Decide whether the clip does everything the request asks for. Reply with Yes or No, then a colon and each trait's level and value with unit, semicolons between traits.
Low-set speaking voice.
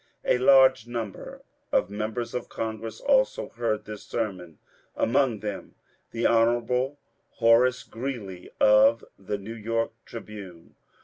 Yes: low, 115 Hz